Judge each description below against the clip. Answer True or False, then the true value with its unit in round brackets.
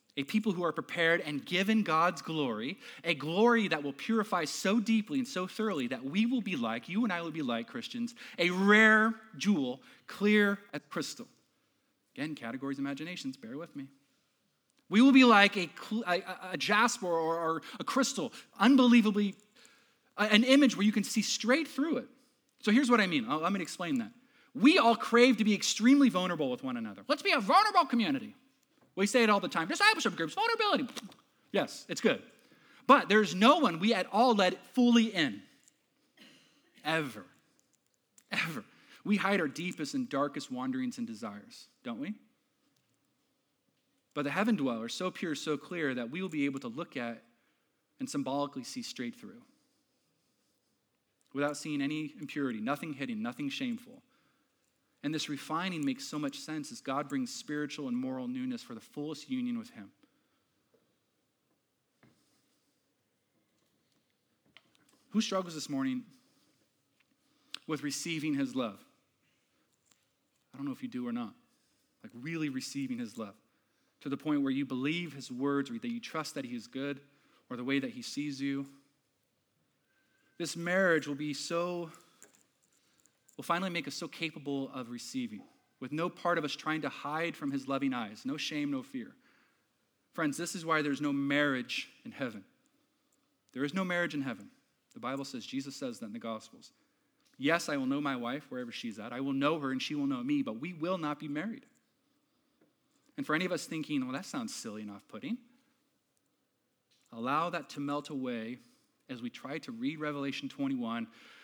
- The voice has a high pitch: True (215 Hz)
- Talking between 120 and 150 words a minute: False (170 wpm)